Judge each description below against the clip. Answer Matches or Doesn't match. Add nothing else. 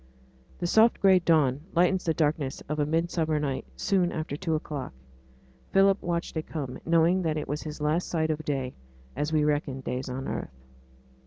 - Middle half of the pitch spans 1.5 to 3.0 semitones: Matches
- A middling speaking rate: Matches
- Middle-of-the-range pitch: Matches